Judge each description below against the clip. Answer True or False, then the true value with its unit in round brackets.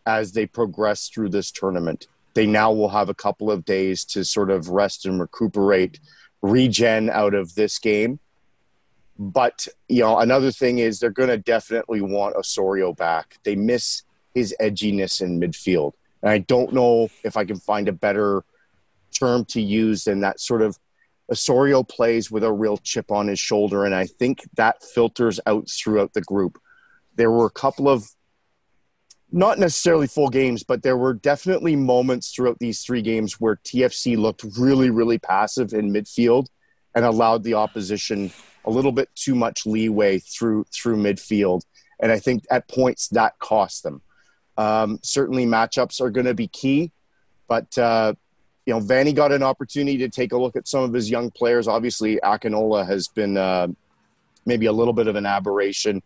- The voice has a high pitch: False (110 Hz)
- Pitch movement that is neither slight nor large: True (3.3 semitones)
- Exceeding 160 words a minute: True (175 wpm)